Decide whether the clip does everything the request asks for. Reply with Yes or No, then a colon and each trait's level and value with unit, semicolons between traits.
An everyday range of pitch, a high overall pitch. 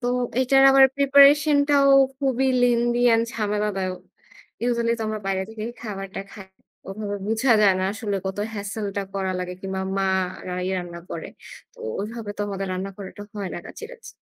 Yes: average, 3.9 semitones; high, 210 Hz